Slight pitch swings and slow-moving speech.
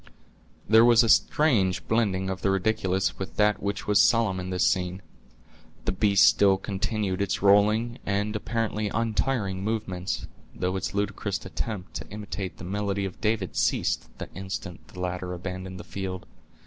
No: narrow, 2.3 semitones; average, 160 wpm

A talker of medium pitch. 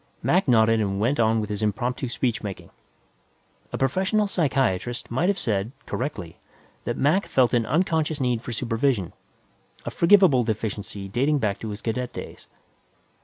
No: low, 120 Hz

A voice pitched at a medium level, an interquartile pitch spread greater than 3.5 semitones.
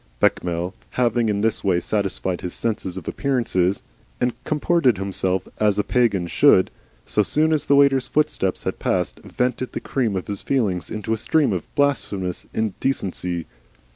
No: low, 105 Hz; wide, 5.6 semitones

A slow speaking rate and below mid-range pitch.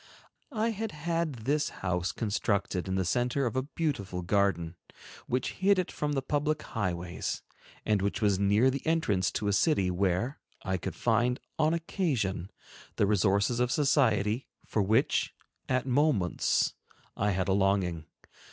No: average, 155 wpm; low, 110 Hz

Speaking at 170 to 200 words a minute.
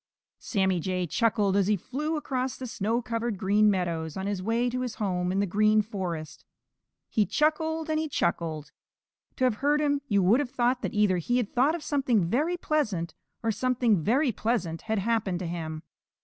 Yes: average, 195 wpm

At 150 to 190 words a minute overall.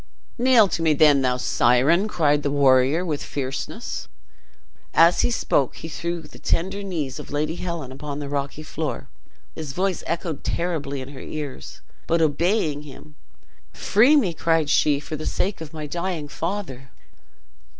Yes: average, 160 wpm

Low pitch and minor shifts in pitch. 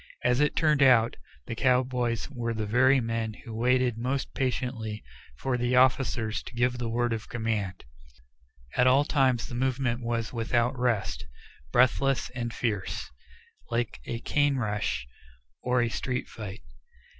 Yes: low, 120 Hz; narrow, 2.1 semitones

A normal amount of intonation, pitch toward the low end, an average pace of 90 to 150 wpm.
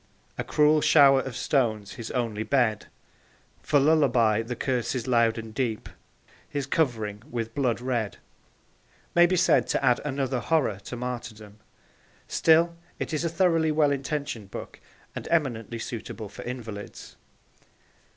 Yes: average, 4.5 semitones; low, 125 Hz; average, 140 wpm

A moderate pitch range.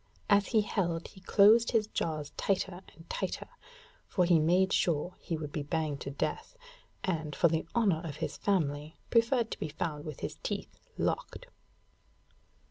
Yes: average, 4.5 semitones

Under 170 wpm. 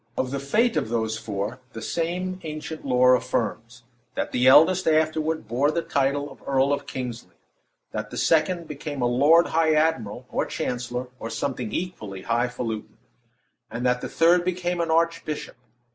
Yes: average, 160 wpm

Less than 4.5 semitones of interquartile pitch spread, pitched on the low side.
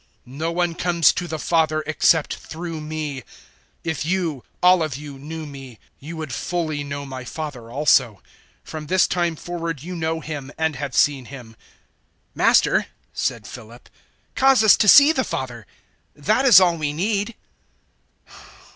No: average, 3.8 semitones; medium, 155 Hz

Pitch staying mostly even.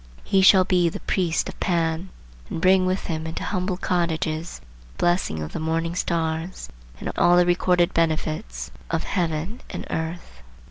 Yes: narrow, 2.1 semitones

